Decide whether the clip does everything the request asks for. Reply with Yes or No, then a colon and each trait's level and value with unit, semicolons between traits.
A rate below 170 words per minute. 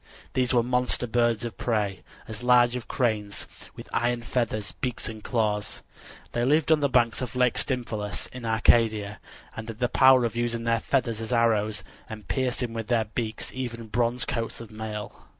No: average, 180 wpm